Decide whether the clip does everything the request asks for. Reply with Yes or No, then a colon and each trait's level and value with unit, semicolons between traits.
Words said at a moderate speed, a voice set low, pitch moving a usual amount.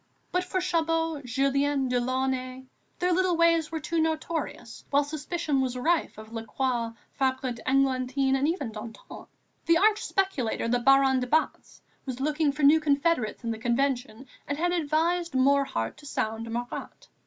No: average, 155 wpm; very high, 275 Hz; average, 4.4 semitones